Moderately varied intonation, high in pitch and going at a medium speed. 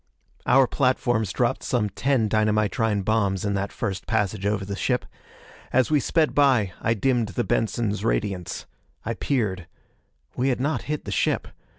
No: average, 4.2 semitones; low, 110 Hz; average, 160 wpm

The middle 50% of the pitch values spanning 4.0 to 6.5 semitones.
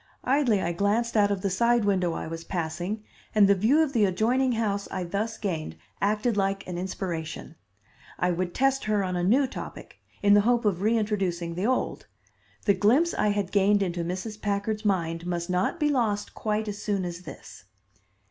No: average, 3.4 semitones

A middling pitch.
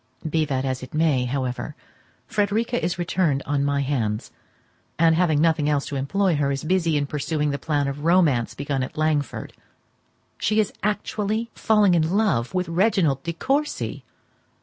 Yes: medium, 155 Hz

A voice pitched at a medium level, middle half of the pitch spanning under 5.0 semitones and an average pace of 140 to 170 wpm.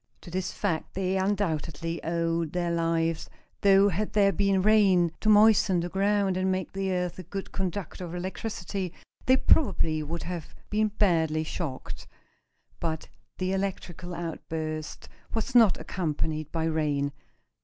Yes: medium, 180 Hz; average, 3.1 semitones; average, 145 wpm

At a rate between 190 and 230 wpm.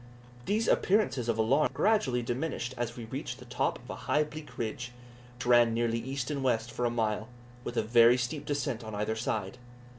Yes: fast, 205 wpm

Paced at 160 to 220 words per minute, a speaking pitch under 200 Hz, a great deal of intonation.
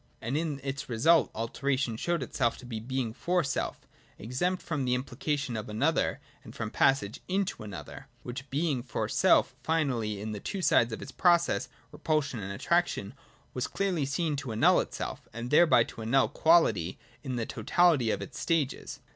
Yes: average, 170 wpm; low, 135 Hz; wide, 5.9 semitones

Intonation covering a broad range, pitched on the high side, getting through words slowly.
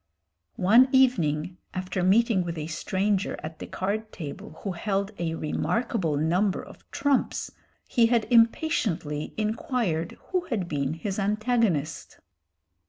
Yes: wide, 5.8 semitones; high, 195 Hz; slow, 125 wpm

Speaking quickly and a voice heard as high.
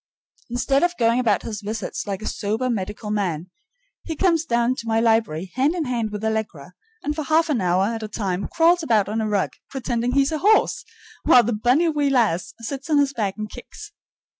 Yes: fast, 210 wpm; high, 230 Hz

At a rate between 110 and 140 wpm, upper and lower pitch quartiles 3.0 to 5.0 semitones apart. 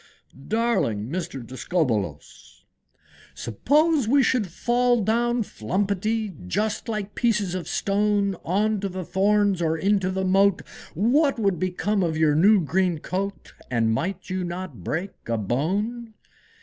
Yes: slow, 135 wpm; average, 4.5 semitones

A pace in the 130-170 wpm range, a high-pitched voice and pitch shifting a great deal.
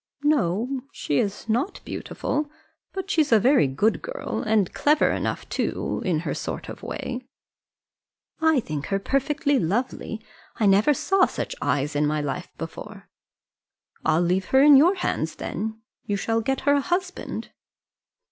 Yes: average, 150 wpm; high, 230 Hz; wide, 7.7 semitones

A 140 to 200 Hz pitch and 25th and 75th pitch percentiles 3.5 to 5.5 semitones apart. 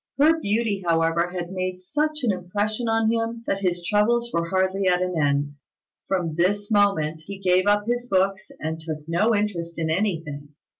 Yes: high, 190 Hz; average, 3.9 semitones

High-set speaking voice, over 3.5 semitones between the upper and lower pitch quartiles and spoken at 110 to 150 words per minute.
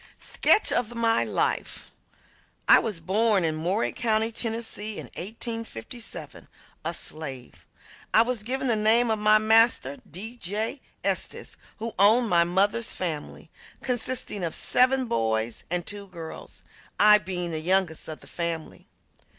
Yes: high, 210 Hz; average, 5.1 semitones; average, 140 wpm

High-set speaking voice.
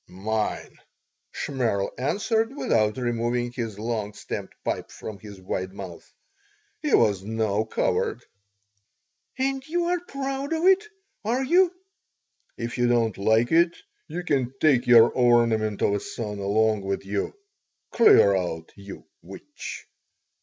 No: low, 115 Hz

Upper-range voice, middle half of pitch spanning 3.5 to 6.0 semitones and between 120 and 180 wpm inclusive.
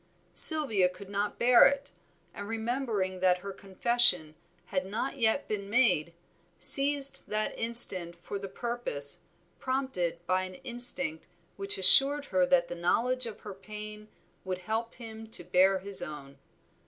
Yes: high, 210 Hz; average, 4.7 semitones; average, 145 wpm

